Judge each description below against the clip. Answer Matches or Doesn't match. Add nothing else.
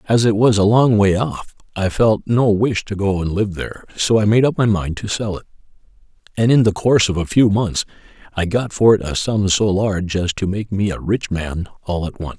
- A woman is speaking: Doesn't match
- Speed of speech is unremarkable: Doesn't match